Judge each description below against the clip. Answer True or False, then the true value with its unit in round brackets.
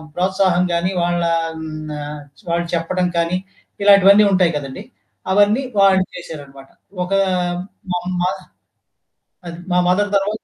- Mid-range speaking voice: True (180 Hz)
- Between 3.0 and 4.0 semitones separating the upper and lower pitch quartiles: False (2.4 semitones)